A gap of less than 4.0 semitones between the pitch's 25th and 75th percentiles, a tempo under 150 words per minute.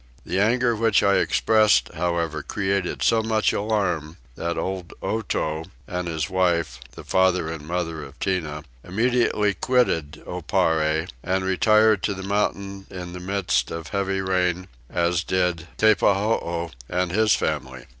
Yes: average, 3.2 semitones; average, 140 wpm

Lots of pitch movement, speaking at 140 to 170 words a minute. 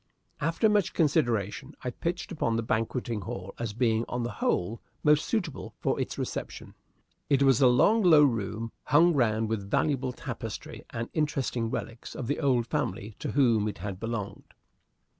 No: average, 4.8 semitones; average, 165 wpm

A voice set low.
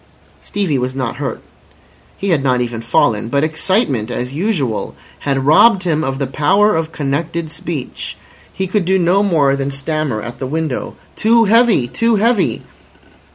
No: medium, 155 Hz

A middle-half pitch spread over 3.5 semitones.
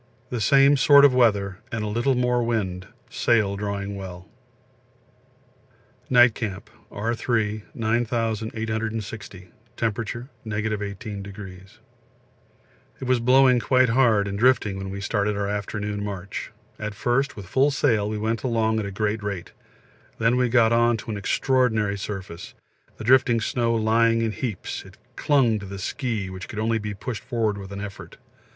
No: average, 2.7 semitones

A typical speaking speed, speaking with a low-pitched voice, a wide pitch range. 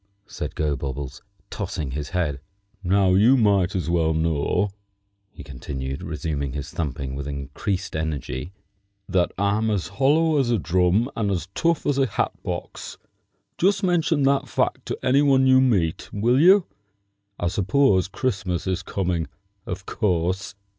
Yes: average, 145 wpm; very low, 95 Hz; wide, 7.5 semitones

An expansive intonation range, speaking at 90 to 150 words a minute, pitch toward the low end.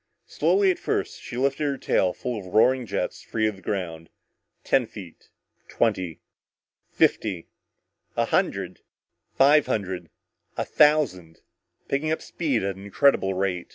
Yes: wide, 6.9 semitones; average, 140 wpm; low, 110 Hz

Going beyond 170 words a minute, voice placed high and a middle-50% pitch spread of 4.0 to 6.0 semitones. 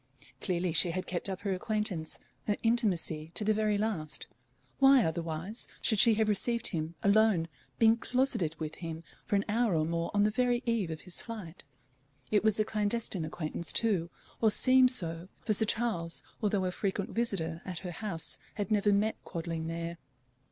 Yes: average, 180 wpm; high, 200 Hz; average, 4.6 semitones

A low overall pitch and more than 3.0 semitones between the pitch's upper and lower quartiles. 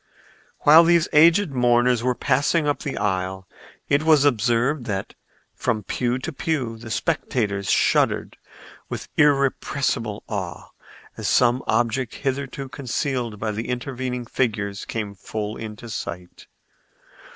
Yes: low, 120 Hz; average, 4.5 semitones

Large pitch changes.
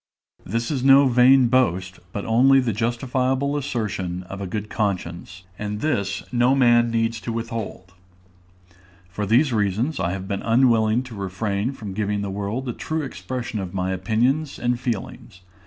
No: average, 4.2 semitones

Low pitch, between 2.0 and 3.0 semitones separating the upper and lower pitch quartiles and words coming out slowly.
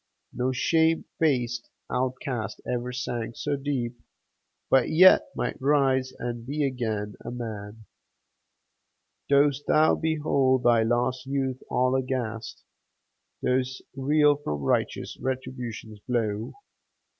Yes: low, 130 Hz; average, 2.7 semitones; slow, 110 wpm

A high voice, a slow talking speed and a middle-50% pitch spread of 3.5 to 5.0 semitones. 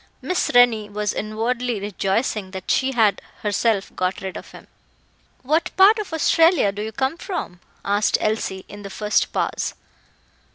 No: high, 215 Hz; average, 155 wpm; average, 4.6 semitones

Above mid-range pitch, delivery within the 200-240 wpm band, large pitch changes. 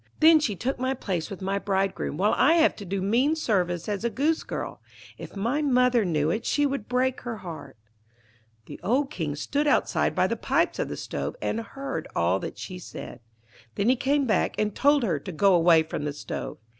Yes: high, 210 Hz; fast, 205 wpm; wide, 7.0 semitones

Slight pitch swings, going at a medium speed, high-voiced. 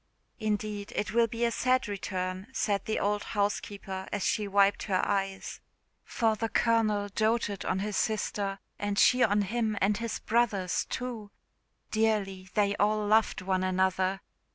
Yes: narrow, 2.0 semitones; average, 155 wpm; high, 205 Hz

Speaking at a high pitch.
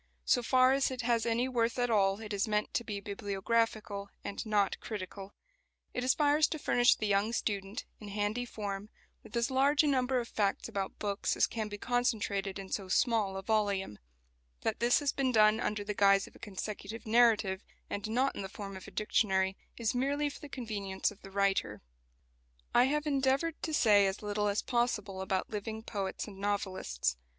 Yes: high, 215 Hz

